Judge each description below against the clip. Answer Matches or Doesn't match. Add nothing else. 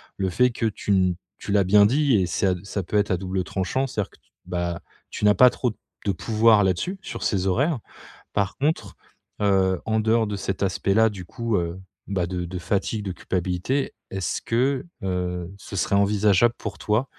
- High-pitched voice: Doesn't match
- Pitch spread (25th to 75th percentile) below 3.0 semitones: Doesn't match